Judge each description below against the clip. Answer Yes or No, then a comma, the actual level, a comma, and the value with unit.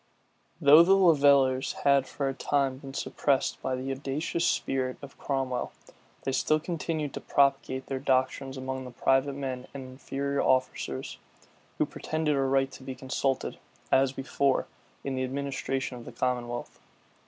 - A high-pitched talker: No, low, 135 Hz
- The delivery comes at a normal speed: Yes, average, 155 wpm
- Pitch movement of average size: No, narrow, 1.3 semitones